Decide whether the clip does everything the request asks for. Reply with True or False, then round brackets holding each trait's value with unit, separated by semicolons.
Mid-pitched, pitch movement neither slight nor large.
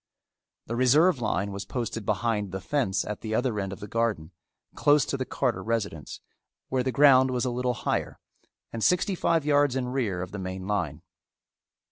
False (115 Hz; 4.4 semitones)